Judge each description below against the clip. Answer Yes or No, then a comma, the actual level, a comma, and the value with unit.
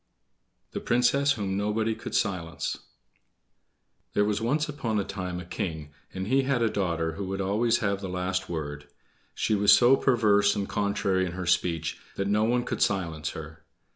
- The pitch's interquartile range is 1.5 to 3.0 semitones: No, average, 4.0 semitones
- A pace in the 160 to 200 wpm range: Yes, average, 175 wpm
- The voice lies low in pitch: Yes, low, 100 Hz